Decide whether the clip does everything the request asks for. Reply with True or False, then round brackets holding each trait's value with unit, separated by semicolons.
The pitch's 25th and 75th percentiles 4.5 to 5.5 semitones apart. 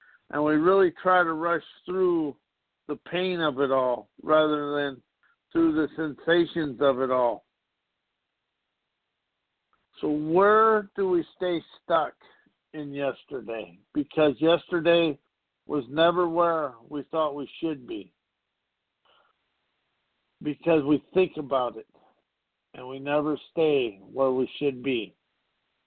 False (3.3 semitones)